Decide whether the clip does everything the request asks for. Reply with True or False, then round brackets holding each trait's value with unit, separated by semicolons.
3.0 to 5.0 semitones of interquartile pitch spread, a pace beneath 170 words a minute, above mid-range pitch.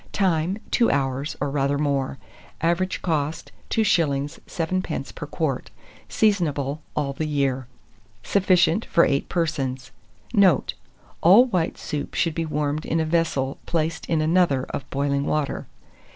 False (3.5 semitones; 135 wpm; 155 Hz)